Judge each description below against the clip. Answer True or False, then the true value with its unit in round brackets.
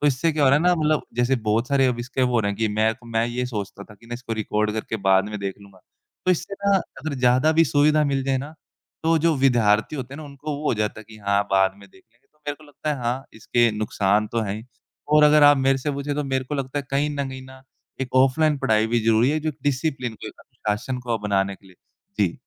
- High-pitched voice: False (130 Hz)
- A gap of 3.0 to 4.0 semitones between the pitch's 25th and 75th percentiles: False (4.9 semitones)